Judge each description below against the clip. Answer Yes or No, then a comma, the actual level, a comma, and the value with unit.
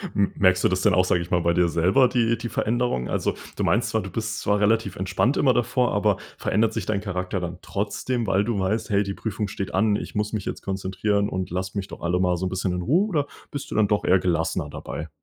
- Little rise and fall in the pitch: No, average, 3.3 semitones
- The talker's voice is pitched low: Yes, low, 100 Hz